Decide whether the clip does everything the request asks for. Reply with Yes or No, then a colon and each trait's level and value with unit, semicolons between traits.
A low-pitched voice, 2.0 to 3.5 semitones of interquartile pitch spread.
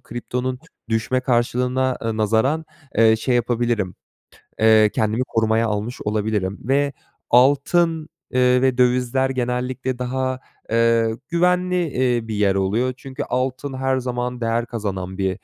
Yes: low, 125 Hz; narrow, 2.6 semitones